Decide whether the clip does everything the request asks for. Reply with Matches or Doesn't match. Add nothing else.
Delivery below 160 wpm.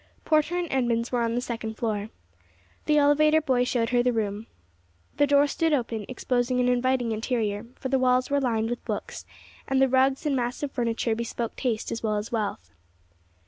Doesn't match